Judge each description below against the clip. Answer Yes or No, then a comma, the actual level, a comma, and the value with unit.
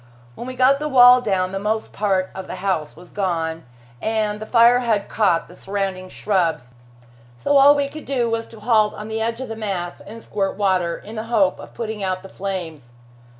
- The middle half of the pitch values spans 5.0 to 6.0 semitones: No, average, 3.7 semitones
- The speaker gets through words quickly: Yes, fast, 210 wpm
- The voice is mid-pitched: No, high, 210 Hz